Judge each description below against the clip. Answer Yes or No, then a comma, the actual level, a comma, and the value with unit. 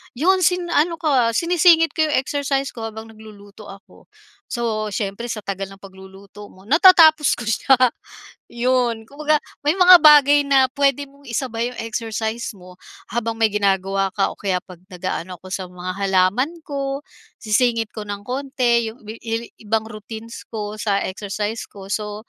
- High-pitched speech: Yes, high, 225 Hz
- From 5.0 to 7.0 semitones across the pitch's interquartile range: Yes, average, 5.3 semitones